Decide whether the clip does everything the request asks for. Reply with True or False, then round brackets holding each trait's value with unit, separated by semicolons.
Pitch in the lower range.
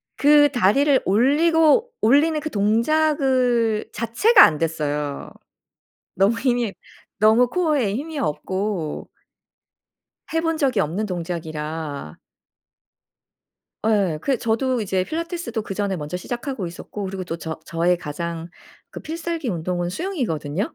False (215 Hz)